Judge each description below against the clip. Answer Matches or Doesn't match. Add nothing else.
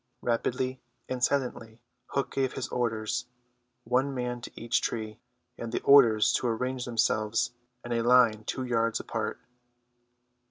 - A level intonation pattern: Matches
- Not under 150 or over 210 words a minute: Doesn't match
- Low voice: Matches